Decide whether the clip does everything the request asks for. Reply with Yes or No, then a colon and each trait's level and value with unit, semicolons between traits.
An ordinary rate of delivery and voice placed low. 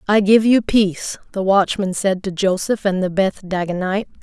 No: average, 185 wpm; high, 195 Hz